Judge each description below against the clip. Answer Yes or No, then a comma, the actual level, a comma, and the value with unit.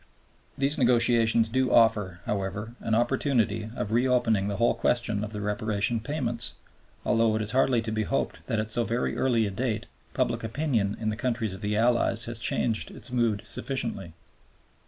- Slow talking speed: No, average, 175 wpm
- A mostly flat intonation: Yes, narrow, 2.2 semitones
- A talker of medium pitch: No, low, 115 Hz